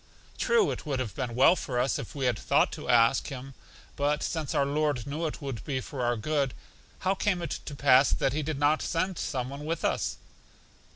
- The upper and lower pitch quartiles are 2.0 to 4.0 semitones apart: Yes, average, 3.2 semitones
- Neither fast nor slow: No, fast, 220 wpm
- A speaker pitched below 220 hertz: Yes, medium, 140 Hz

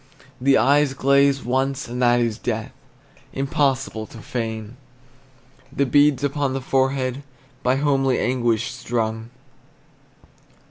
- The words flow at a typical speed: No, slow, 110 wpm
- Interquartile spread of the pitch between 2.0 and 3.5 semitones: Yes, narrow, 2.4 semitones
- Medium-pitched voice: No, low, 130 Hz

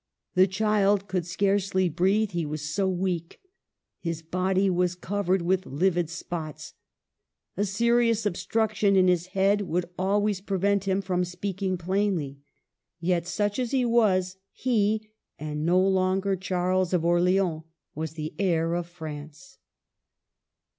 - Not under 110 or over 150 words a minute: Yes, slow, 135 wpm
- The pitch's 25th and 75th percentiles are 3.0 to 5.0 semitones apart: No, narrow, 2.6 semitones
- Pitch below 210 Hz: Yes, medium, 185 Hz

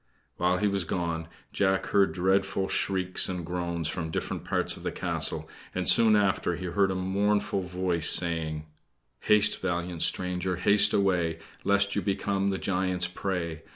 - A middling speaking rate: Yes, average, 155 wpm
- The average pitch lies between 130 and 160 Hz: No, very low, 95 Hz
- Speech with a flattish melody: Yes, narrow, 2.1 semitones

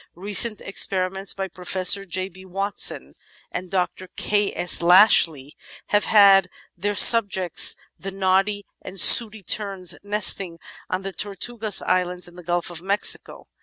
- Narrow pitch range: Yes, narrow, 2.0 semitones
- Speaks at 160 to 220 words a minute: No, average, 150 wpm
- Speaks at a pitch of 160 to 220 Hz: Yes, high, 190 Hz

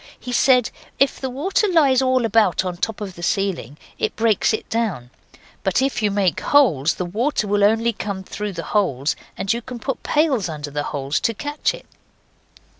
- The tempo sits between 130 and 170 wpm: No, average, 195 wpm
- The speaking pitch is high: Yes, high, 215 Hz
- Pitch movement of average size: No, wide, 5.8 semitones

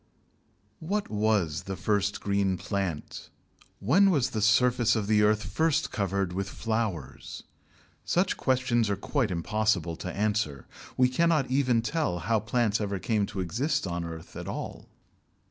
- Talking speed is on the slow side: No, average, 150 wpm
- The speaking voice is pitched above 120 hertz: No, low, 105 Hz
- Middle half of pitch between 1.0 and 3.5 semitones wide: No, average, 4.4 semitones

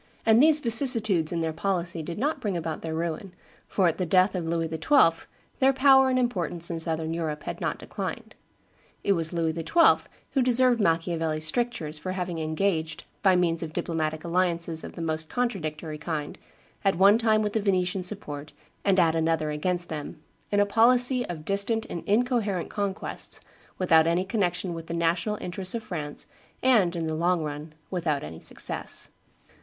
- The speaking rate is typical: Yes, average, 175 wpm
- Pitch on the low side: No, medium, 175 Hz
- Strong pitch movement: No, average, 4.2 semitones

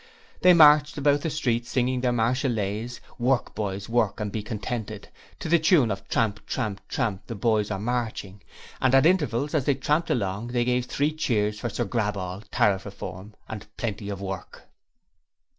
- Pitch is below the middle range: Yes, low, 115 Hz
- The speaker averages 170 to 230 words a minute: Yes, average, 175 wpm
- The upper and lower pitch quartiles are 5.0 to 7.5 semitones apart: No, average, 4.1 semitones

